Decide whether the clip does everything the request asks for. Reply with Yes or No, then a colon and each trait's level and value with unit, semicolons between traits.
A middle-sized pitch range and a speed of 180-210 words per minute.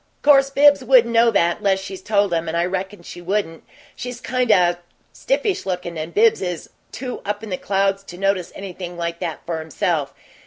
Yes: average, 4.7 semitones; average, 195 wpm